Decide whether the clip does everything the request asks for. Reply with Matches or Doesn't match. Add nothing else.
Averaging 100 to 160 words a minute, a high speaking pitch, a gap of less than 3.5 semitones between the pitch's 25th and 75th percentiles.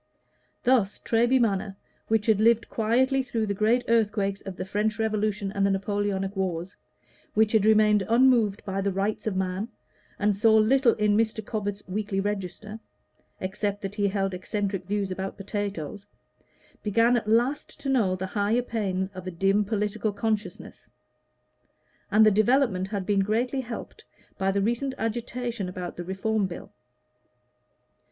Matches